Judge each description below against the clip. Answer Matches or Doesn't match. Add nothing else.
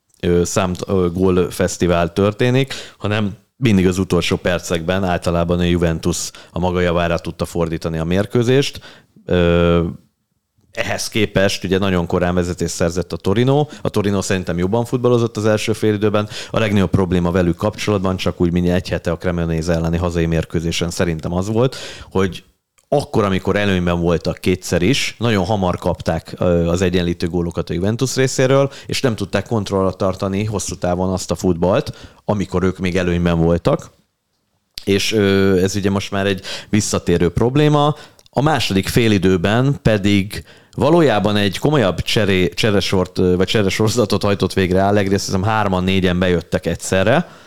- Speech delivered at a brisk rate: Doesn't match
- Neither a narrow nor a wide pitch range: Matches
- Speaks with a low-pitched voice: Matches